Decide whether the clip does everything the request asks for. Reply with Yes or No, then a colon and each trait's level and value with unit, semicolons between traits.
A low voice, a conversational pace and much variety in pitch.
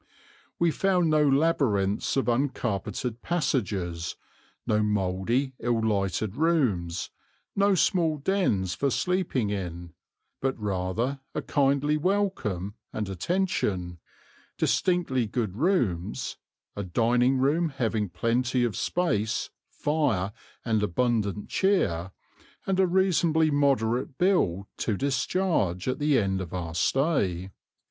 No: low, 120 Hz; slow, 110 wpm; wide, 7.8 semitones